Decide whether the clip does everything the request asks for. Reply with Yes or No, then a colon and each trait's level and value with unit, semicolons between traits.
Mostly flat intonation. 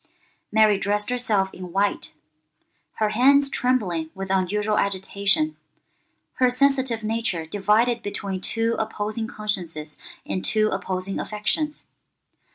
No: average, 3.2 semitones